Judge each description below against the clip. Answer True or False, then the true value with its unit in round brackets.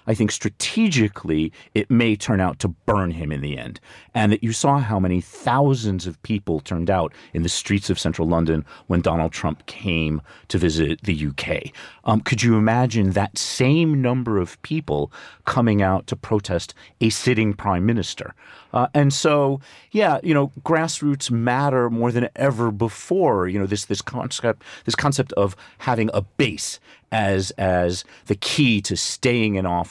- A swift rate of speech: False (175 wpm)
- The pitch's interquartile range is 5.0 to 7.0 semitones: True (5.5 semitones)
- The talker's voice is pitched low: True (105 Hz)